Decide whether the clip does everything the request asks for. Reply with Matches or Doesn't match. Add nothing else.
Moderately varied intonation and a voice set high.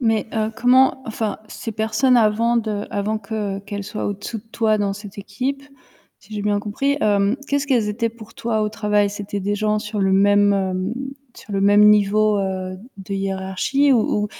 Doesn't match